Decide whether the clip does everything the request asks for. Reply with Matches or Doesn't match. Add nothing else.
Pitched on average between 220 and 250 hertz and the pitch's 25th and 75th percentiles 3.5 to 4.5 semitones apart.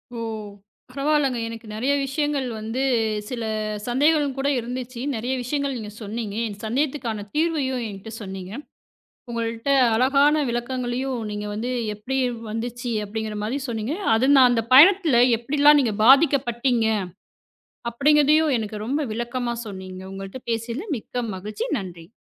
Matches